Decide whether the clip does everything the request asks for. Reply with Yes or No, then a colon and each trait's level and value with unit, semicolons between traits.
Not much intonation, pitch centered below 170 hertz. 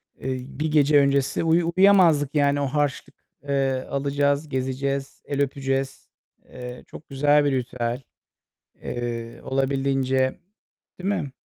Yes: narrow, 1.7 semitones; medium, 140 Hz